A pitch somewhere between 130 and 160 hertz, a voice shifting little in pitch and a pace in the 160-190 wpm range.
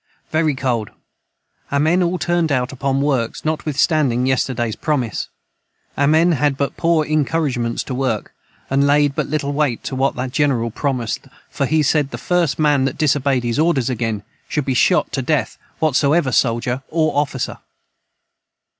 No: medium, 140 Hz; average, 3.3 semitones; average, 165 wpm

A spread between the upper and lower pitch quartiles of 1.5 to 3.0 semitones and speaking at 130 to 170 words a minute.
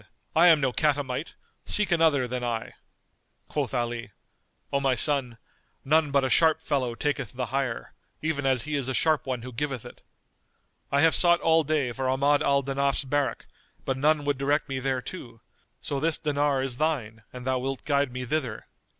No: average, 2.7 semitones; average, 185 wpm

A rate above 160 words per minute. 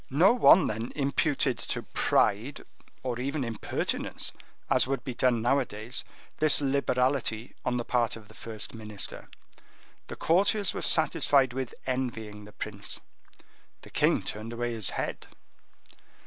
No: slow, 135 wpm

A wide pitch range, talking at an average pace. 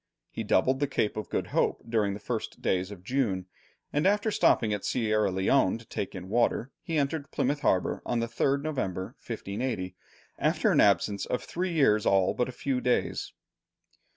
Yes: wide, 5.8 semitones; average, 180 wpm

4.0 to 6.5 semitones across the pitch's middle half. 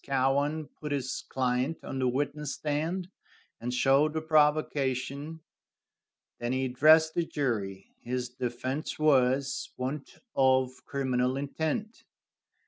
No: average, 3.0 semitones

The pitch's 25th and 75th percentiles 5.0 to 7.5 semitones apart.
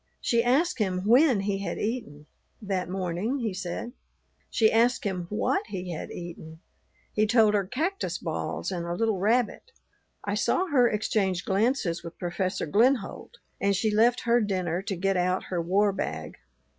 No: average, 4.4 semitones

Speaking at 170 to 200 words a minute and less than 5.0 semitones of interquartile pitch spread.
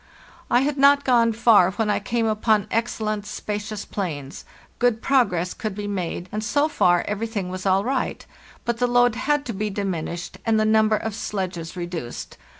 Yes: average, 175 wpm; average, 3.9 semitones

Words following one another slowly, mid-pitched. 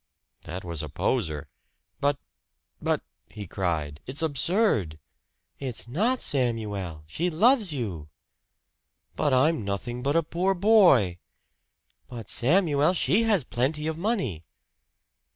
No: slow, 120 wpm; low, 130 Hz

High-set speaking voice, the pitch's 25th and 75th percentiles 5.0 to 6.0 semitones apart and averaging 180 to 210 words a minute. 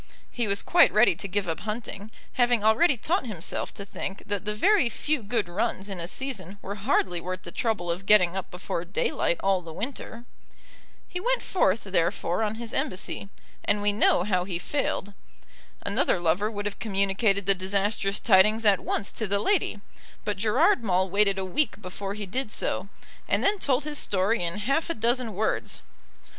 No: high, 205 Hz; average, 3.5 semitones; average, 185 wpm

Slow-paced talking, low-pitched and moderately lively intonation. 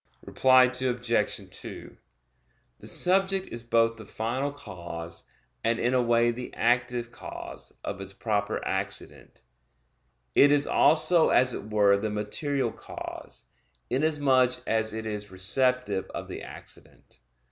Yes: slow, 130 wpm; low, 120 Hz; average, 3.5 semitones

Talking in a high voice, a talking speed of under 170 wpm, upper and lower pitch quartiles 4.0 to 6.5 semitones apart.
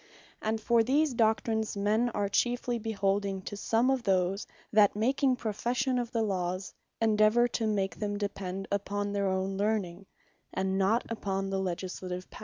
No: high, 205 Hz; average, 160 wpm; average, 2.8 semitones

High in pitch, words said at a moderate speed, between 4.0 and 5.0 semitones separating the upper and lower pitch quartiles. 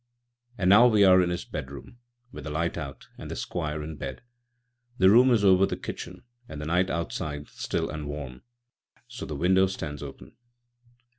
No: very low, 85 Hz; average, 180 wpm; average, 4.4 semitones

